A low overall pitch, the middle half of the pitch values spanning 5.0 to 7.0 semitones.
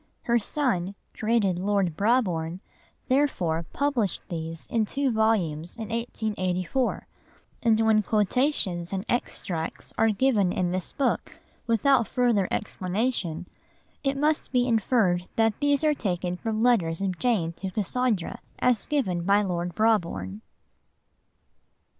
No: high, 210 Hz; average, 5.3 semitones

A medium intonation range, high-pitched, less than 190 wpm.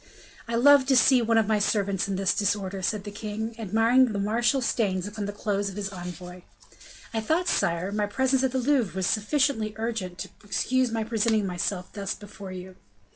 No: average, 3.1 semitones; high, 210 Hz; average, 195 wpm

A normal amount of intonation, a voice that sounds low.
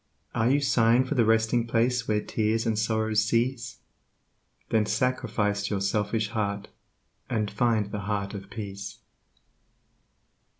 No: narrow, 2.1 semitones; low, 110 Hz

